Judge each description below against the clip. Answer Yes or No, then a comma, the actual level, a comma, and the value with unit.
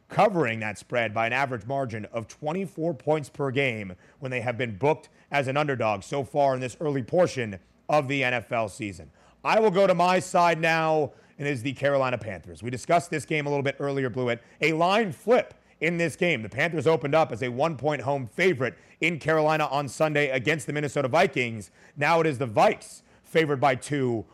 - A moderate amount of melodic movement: Yes, average, 4.1 semitones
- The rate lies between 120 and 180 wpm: No, fast, 205 wpm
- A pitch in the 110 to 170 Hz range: Yes, medium, 140 Hz